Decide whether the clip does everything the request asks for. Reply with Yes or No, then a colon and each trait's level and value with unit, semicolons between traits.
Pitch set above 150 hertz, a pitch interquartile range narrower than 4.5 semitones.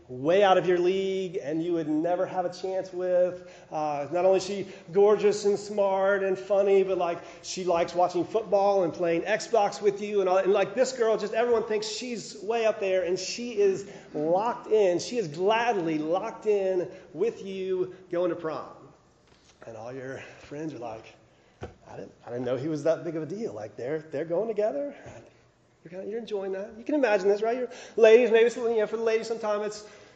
Yes: high, 190 Hz; average, 3.5 semitones